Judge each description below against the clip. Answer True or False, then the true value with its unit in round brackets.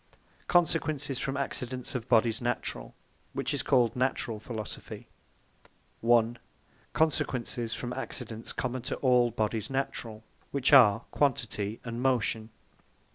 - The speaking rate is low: True (120 wpm)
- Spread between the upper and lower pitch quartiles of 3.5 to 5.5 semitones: False (2.9 semitones)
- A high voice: False (120 Hz)